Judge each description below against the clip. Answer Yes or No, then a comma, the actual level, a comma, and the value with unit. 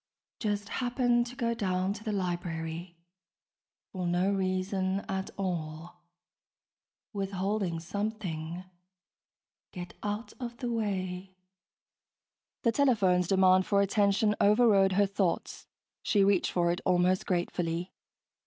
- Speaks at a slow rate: Yes, slow, 110 wpm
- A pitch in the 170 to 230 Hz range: Yes, high, 190 Hz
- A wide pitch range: No, narrow, 2.6 semitones